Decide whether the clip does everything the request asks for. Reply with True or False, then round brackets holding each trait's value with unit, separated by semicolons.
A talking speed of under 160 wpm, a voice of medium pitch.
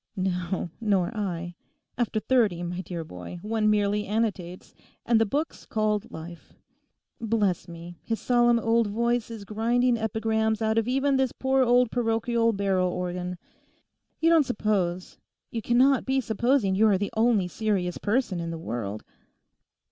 False (150 wpm; 215 Hz)